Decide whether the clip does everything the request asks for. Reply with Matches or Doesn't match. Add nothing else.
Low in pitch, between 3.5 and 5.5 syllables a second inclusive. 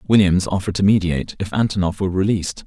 Doesn't match